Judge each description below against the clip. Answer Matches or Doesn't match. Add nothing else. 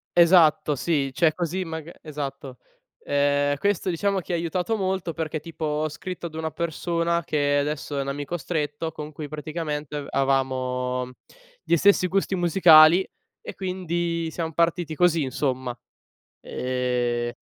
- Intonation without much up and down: Doesn't match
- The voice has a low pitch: Doesn't match